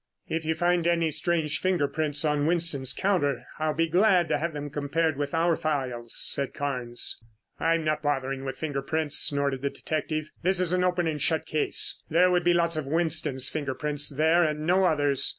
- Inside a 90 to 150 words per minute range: No, average, 200 wpm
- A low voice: No, medium, 155 Hz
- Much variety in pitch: No, average, 2.9 semitones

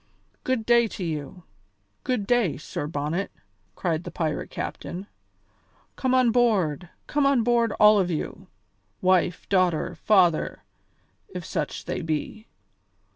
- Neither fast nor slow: No, slow, 130 wpm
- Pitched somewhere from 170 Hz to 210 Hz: Yes, high, 190 Hz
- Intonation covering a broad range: Yes, wide, 6.1 semitones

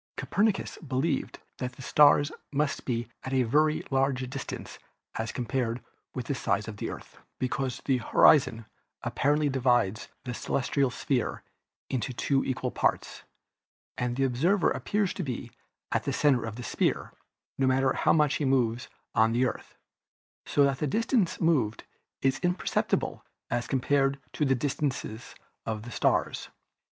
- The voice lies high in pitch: No, low, 135 Hz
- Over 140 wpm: Yes, average, 150 wpm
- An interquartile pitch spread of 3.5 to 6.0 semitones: No, average, 3.0 semitones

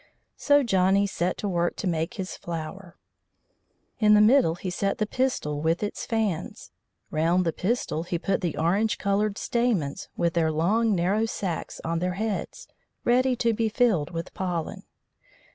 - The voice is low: No, high, 190 Hz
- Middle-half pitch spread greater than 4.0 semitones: Yes, average, 4.5 semitones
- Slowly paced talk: No, average, 160 wpm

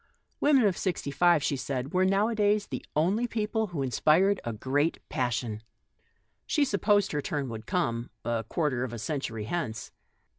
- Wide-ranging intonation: Yes, wide, 8.3 semitones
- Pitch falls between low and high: Yes, medium, 150 Hz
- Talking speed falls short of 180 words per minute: Yes, average, 170 wpm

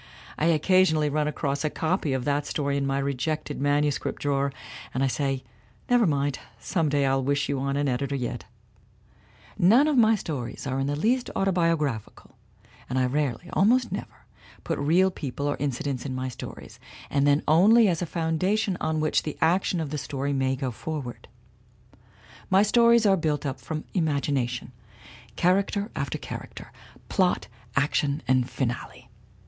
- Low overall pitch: No, medium, 145 Hz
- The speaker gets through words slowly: No, average, 170 wpm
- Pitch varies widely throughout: No, average, 4.0 semitones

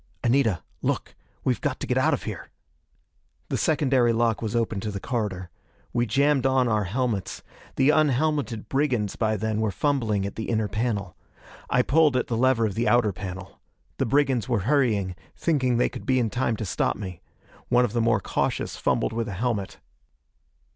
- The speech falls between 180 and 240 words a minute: Yes, average, 185 wpm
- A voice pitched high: No, low, 115 Hz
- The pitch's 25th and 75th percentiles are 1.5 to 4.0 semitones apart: Yes, average, 3.7 semitones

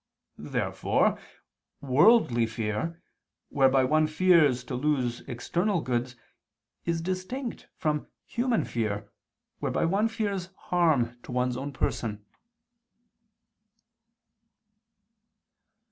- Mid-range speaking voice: Yes, medium, 145 Hz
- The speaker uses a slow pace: Yes, slow, 85 wpm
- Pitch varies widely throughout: Yes, wide, 6.7 semitones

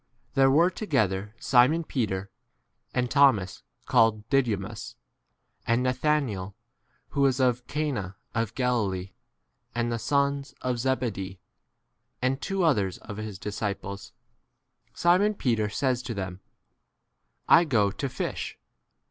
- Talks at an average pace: No, slow, 120 wpm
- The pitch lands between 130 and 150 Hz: No, low, 120 Hz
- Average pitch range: Yes, average, 5.0 semitones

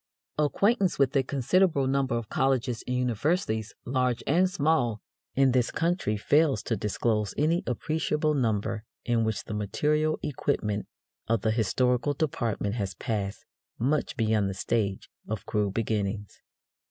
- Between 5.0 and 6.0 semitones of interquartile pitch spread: Yes, average, 5.3 semitones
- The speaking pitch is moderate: No, low, 120 Hz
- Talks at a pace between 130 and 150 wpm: Yes, average, 140 wpm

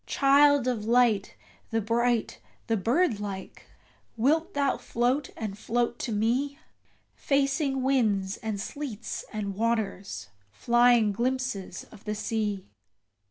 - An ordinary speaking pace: No, slow, 115 wpm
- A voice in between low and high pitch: No, high, 235 Hz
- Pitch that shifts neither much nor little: Yes, average, 4.0 semitones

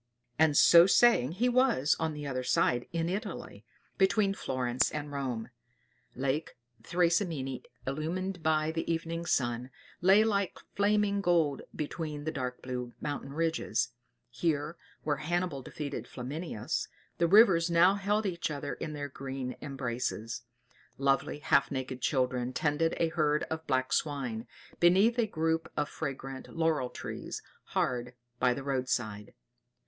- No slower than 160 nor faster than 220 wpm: No, average, 140 wpm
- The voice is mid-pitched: Yes, medium, 150 Hz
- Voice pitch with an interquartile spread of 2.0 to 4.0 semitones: No, average, 4.6 semitones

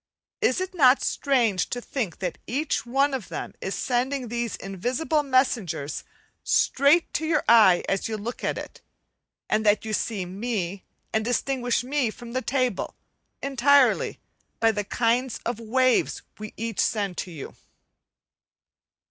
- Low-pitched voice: No, high, 240 Hz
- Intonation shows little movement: No, average, 4.0 semitones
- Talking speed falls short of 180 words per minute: Yes, average, 150 wpm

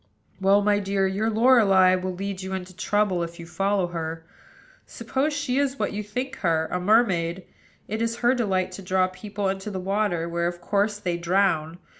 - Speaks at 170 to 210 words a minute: Yes, average, 190 wpm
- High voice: Yes, high, 195 Hz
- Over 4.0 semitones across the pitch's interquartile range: No, average, 2.8 semitones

